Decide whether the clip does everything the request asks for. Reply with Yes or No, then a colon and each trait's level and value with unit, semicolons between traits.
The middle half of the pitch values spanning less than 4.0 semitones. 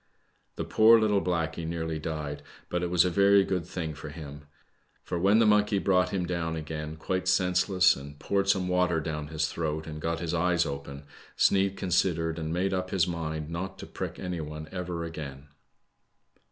Yes: average, 2.8 semitones